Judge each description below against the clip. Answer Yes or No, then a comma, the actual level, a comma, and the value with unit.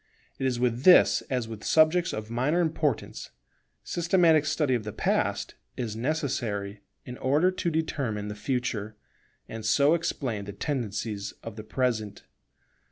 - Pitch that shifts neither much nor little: No, wide, 6.1 semitones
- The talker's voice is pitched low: Yes, low, 125 Hz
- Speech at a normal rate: Yes, average, 145 wpm